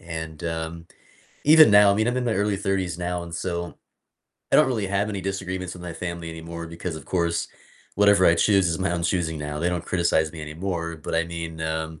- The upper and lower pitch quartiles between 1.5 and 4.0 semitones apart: Yes, average, 2.7 semitones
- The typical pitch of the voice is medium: No, very low, 85 Hz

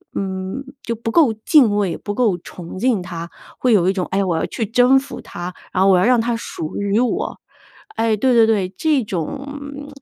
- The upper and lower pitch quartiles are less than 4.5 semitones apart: No, average, 5.1 semitones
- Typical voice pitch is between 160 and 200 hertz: No, high, 220 Hz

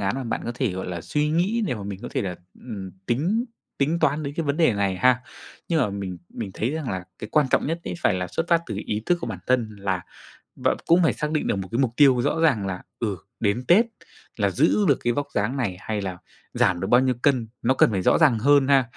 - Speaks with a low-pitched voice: Yes, low, 125 Hz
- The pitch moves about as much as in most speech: No, wide, 7.0 semitones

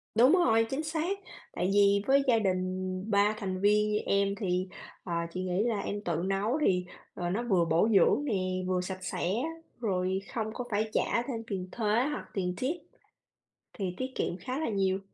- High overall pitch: Yes, high, 200 Hz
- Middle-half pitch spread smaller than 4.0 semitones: Yes, average, 3.6 semitones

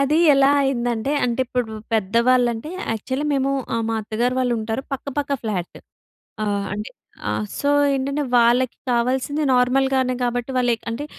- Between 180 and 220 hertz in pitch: No, very high, 250 Hz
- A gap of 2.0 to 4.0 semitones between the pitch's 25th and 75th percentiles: Yes, average, 2.7 semitones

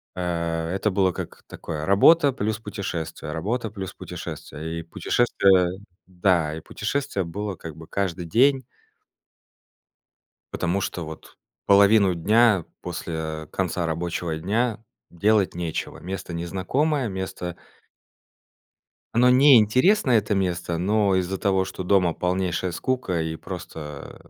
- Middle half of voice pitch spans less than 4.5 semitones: Yes, average, 4.0 semitones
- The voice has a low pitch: Yes, very low, 95 Hz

